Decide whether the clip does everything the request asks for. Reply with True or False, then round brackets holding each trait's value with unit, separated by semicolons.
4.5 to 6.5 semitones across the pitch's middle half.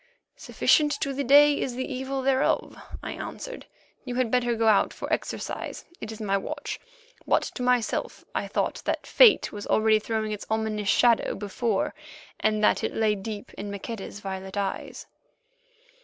False (3.7 semitones)